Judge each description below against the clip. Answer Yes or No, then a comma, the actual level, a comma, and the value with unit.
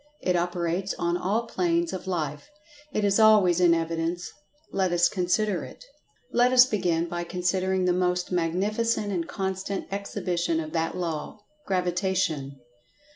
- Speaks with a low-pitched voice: No, medium, 180 Hz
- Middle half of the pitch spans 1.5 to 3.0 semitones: Yes, narrow, 2.4 semitones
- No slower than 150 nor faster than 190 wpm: No, average, 140 wpm